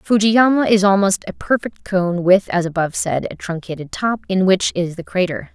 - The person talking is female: Yes, female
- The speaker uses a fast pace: No, average, 195 wpm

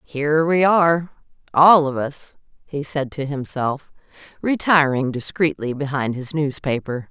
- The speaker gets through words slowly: Yes, slow, 125 wpm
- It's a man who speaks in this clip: No, female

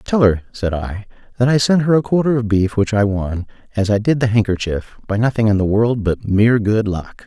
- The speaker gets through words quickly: Yes, fast, 240 wpm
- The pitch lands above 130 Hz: No, low, 110 Hz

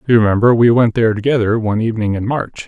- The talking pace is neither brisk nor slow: No, fast, 225 wpm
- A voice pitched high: No, low, 115 Hz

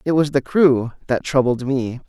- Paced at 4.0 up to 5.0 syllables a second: Yes, 4.5 syllables/s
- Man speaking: Yes, male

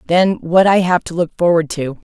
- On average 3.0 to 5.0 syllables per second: Yes, 4.8 syllables/s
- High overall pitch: No, medium, 170 Hz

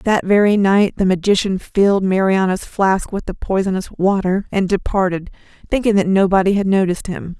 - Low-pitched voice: No, high, 190 Hz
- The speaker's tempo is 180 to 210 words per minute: No, average, 160 wpm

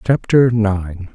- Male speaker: Yes, male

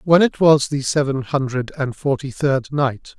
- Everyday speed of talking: Yes, average, 190 wpm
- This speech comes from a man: Yes, male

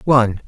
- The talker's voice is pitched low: Yes, low, 120 Hz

